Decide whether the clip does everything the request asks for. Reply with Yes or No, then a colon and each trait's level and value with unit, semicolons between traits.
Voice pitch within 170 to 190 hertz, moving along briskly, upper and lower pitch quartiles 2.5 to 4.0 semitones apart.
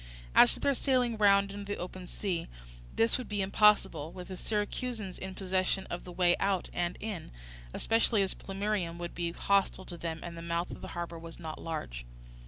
No: medium, 185 Hz; average, 195 wpm; average, 3.1 semitones